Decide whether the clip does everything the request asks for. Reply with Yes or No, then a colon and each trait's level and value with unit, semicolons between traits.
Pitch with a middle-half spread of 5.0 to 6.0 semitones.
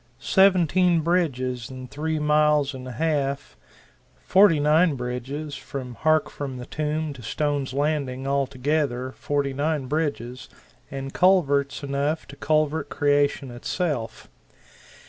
No: average, 2.9 semitones